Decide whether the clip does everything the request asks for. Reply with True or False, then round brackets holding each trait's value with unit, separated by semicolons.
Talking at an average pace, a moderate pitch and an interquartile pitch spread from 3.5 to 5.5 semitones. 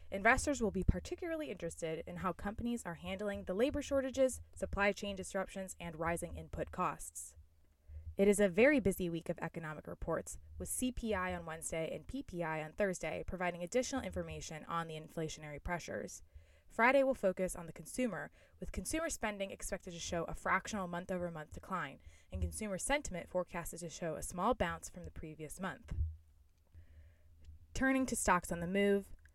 True (165 wpm; 175 Hz; 5.1 semitones)